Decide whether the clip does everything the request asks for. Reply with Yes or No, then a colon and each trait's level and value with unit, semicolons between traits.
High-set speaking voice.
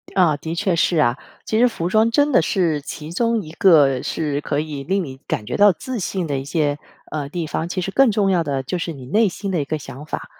No: medium, 165 Hz